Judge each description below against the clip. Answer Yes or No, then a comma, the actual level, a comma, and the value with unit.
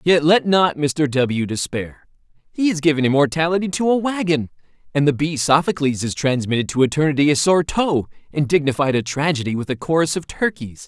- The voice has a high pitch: No, medium, 150 Hz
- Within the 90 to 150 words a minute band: No, average, 180 wpm